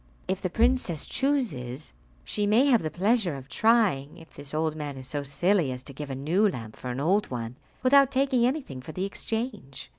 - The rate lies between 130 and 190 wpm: No, fast, 205 wpm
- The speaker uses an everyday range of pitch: No, wide, 8.7 semitones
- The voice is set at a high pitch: No, medium, 170 Hz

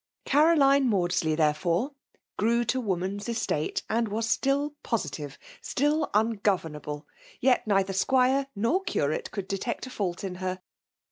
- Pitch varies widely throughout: Yes, wide, 6.2 semitones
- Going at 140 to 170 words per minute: Yes, average, 145 wpm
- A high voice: Yes, high, 215 Hz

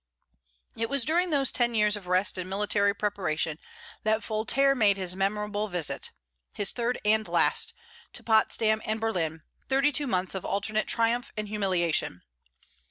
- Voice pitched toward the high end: Yes, high, 210 Hz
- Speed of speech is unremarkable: Yes, average, 155 wpm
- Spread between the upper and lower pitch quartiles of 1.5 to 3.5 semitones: Yes, average, 3.1 semitones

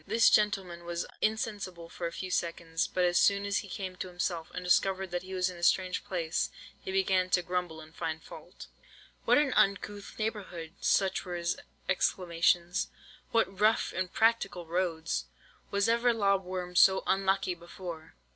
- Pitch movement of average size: No, narrow, 2.3 semitones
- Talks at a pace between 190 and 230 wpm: No, average, 165 wpm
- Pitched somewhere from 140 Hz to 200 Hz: Yes, medium, 185 Hz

